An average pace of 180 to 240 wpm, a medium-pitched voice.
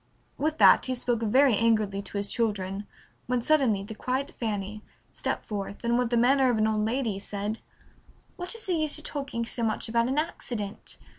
No: average, 195 wpm; high, 230 Hz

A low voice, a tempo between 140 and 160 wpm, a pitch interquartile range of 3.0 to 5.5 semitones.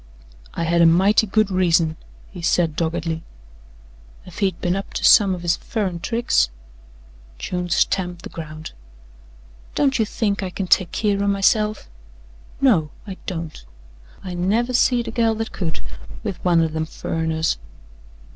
No: medium, 180 Hz; average, 155 wpm; average, 3.9 semitones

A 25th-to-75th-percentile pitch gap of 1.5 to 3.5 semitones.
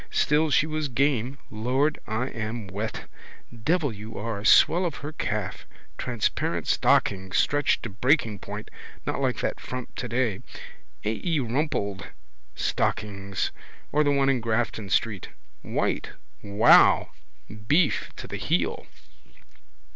No: average, 5.2 semitones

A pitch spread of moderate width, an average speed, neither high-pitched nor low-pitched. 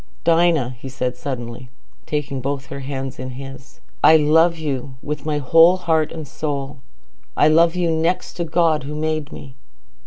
Yes: average, 3.3 semitones; average, 165 wpm; medium, 150 Hz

